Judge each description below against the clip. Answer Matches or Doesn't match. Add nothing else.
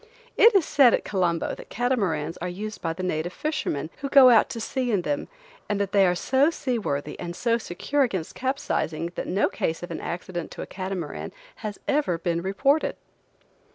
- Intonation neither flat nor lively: Doesn't match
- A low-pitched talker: Doesn't match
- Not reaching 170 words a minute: Doesn't match